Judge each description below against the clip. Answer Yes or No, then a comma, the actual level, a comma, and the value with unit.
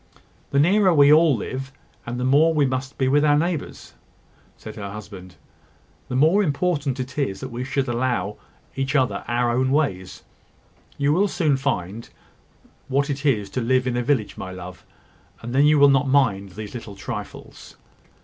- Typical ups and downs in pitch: Yes, average, 3.7 semitones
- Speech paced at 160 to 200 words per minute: Yes, average, 180 wpm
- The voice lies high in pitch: No, low, 130 Hz